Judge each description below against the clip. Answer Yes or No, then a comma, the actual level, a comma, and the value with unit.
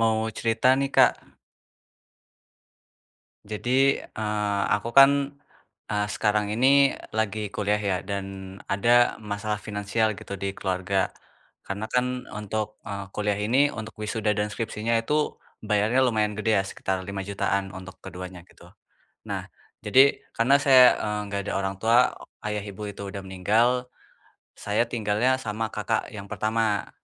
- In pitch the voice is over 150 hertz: No, low, 105 Hz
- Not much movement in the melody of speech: Yes, narrow, 2.0 semitones